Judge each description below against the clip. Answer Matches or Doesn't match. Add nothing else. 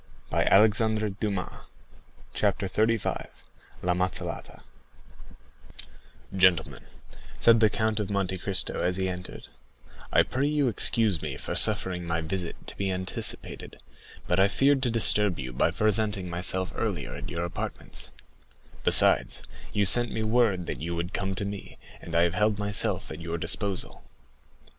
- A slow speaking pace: Doesn't match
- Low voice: Matches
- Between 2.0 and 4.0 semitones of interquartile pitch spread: Matches